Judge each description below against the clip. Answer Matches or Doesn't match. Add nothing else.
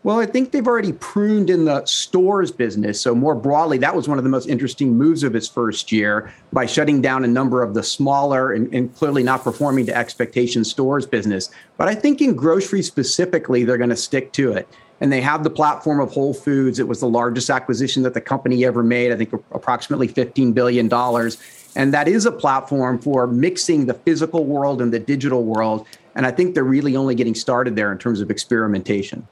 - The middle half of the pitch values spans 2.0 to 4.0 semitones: Matches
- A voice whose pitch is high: Doesn't match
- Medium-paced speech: Doesn't match